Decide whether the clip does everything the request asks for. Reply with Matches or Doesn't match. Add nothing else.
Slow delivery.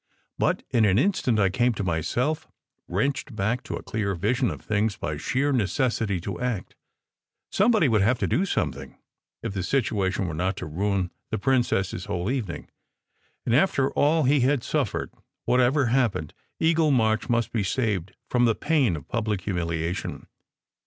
Doesn't match